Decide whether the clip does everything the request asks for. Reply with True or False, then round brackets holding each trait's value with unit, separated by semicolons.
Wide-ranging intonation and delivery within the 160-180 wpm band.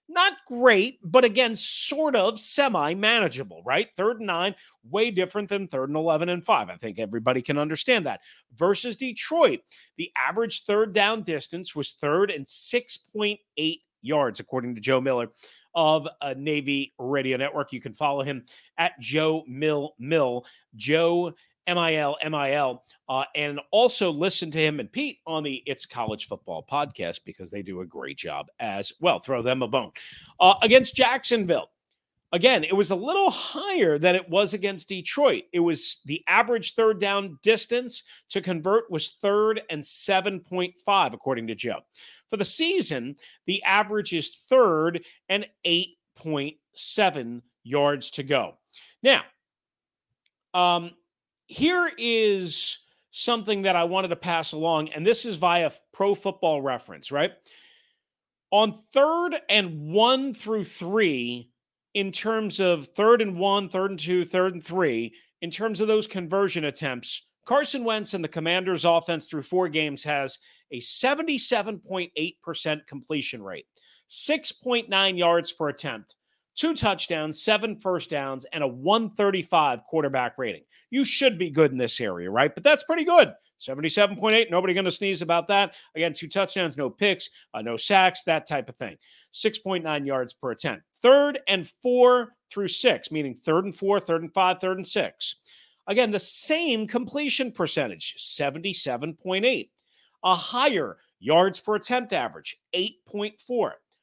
False (6.3 semitones; 150 wpm)